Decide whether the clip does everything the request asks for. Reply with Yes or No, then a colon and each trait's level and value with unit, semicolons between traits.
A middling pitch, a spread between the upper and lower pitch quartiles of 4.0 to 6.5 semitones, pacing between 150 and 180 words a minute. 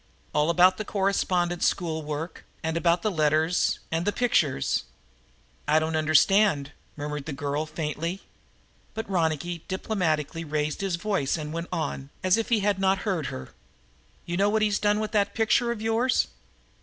Yes: medium, 170 Hz; average, 4.6 semitones; average, 170 wpm